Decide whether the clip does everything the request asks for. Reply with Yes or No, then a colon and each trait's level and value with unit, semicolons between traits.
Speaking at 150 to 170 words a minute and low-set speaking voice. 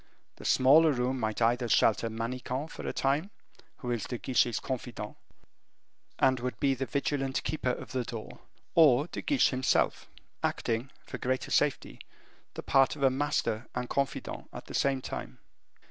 Yes: average, 160 wpm; low, 130 Hz